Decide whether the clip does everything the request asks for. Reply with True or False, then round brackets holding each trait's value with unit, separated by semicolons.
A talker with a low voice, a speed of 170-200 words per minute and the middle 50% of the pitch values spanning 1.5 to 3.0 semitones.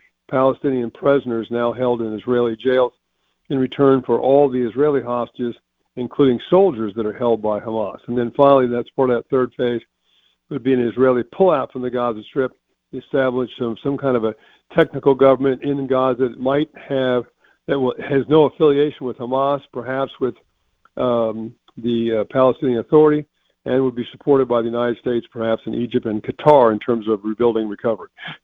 True (125 Hz; 175 wpm; 2.4 semitones)